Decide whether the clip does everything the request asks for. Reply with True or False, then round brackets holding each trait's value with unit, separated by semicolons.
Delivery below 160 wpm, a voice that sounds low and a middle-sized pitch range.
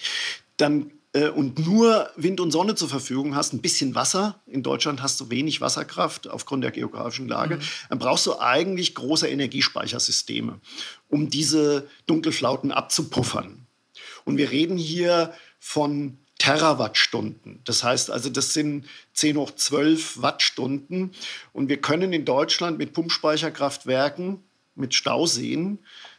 False (130 wpm; 150 Hz; 3.6 semitones)